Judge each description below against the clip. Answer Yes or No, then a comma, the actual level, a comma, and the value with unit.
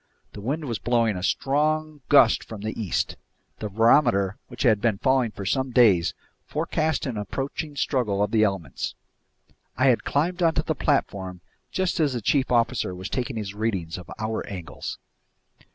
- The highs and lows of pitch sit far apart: Yes, wide, 5.8 semitones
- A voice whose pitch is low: Yes, low, 115 Hz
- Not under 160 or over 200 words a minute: Yes, average, 170 wpm